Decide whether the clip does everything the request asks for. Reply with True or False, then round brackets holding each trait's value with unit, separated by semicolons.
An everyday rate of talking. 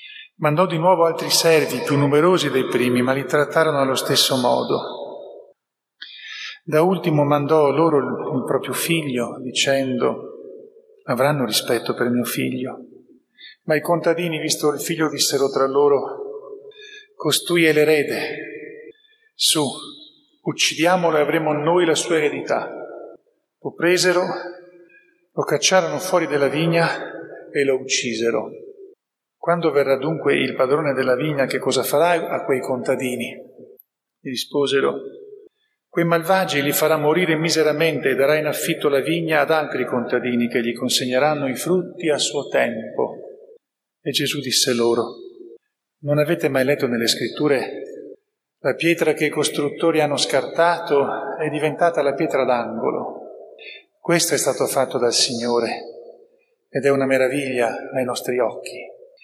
True (135 wpm)